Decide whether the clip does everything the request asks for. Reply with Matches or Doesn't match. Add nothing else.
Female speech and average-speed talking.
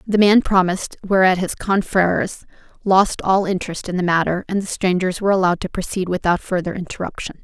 Matches